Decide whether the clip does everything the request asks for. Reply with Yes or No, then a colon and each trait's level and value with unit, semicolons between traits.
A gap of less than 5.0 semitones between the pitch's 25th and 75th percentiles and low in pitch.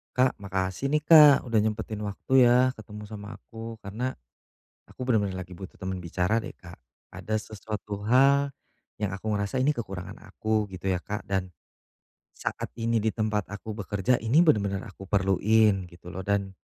Yes: average, 3.0 semitones; low, 105 Hz